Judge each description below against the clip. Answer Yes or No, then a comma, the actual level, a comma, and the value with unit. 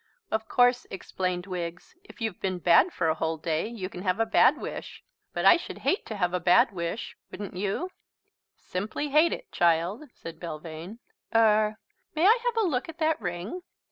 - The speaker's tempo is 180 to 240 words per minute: Yes, average, 190 wpm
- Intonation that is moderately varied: No, wide, 6.2 semitones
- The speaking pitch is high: Yes, high, 200 Hz